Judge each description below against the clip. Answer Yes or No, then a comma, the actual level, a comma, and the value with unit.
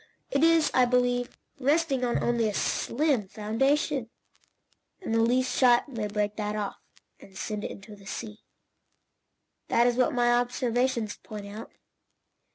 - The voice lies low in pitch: No, high, 240 Hz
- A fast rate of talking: No, average, 150 wpm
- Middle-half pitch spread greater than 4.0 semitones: No, average, 3.3 semitones